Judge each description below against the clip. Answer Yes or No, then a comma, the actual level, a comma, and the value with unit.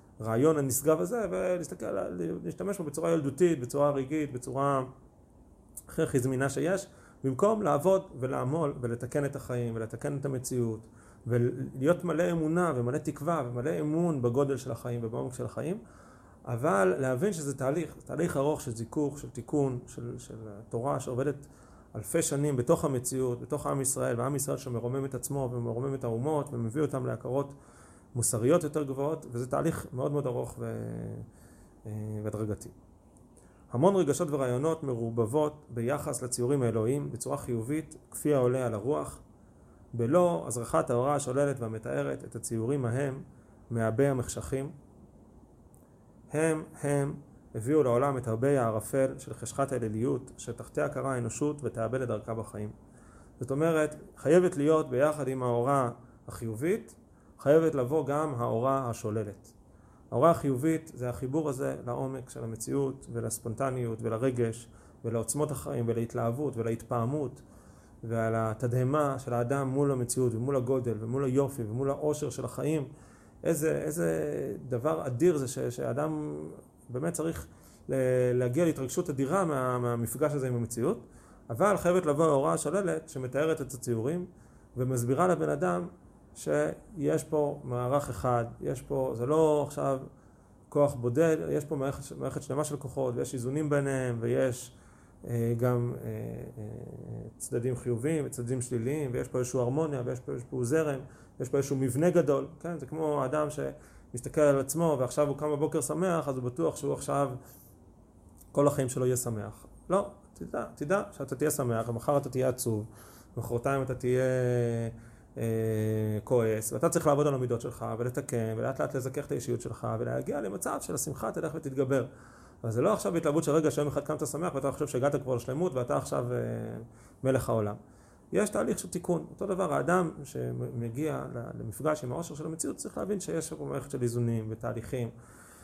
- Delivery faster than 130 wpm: Yes, average, 145 wpm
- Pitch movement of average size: Yes, average, 4.0 semitones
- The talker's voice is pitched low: Yes, low, 130 Hz